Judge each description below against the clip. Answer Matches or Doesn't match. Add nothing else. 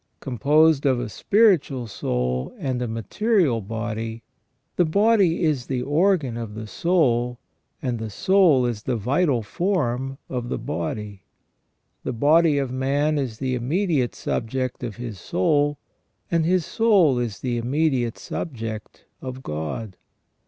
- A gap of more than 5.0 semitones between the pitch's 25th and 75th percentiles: Matches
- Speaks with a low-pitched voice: Matches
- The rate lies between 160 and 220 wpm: Doesn't match